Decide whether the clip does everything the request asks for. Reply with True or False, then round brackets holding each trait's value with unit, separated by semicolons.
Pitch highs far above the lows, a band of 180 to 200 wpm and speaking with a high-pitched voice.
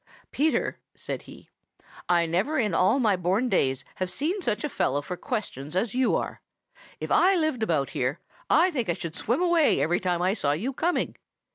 True (8.6 semitones; 190 wpm; 210 Hz)